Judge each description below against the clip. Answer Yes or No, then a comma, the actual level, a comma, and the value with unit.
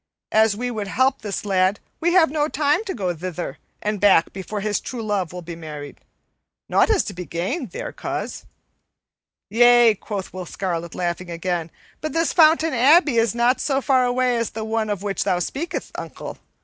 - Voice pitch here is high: Yes, high, 215 Hz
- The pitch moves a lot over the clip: Yes, wide, 5.9 semitones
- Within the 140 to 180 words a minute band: No, average, 190 wpm